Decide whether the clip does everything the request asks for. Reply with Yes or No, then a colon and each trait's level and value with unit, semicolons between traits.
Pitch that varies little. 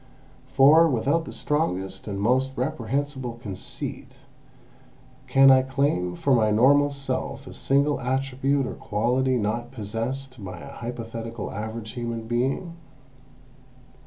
No: average, 3.4 semitones